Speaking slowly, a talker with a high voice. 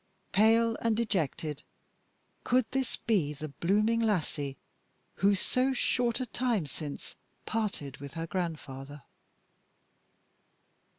Yes: slow, 105 wpm; high, 195 Hz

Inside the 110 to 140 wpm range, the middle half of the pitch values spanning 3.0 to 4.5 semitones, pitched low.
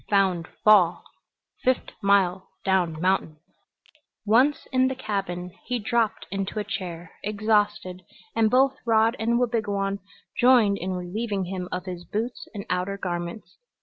No: slow, 135 wpm; average, 3.6 semitones; high, 200 Hz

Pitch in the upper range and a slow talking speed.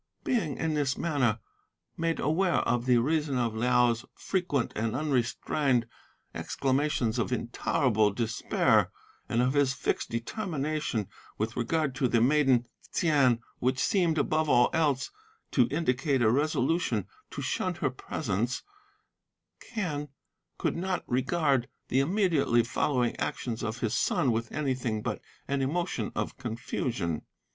No: low, 130 Hz; slow, 130 wpm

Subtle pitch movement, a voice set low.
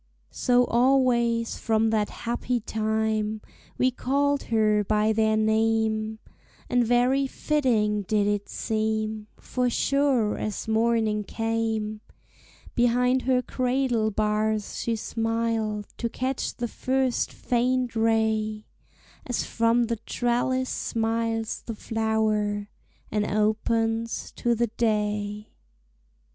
No: narrow, 1.9 semitones; high, 225 Hz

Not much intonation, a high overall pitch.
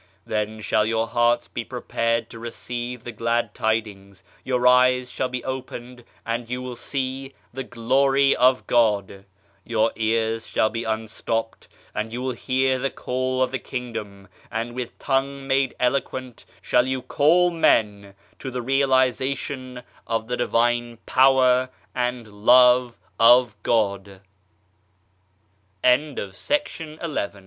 No: narrow, 2.3 semitones; low, 120 Hz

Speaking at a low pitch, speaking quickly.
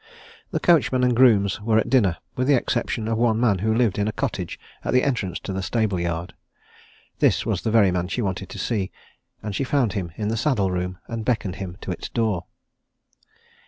Yes: low, 110 Hz; fast, 210 wpm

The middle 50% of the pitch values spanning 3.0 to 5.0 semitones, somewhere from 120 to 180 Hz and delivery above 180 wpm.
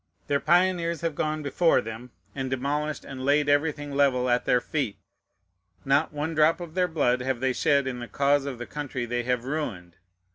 Yes: average, 3.3 semitones; medium, 140 Hz; average, 190 wpm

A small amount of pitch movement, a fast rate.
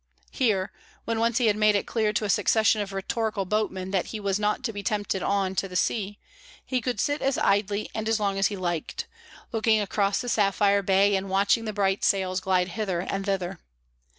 Yes: narrow, 2.1 semitones; fast, 210 wpm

